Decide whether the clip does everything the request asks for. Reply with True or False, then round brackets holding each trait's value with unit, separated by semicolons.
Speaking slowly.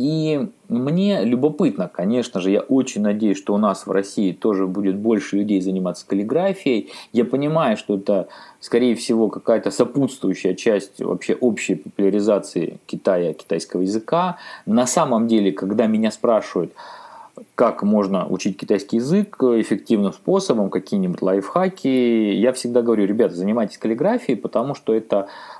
False (135 wpm)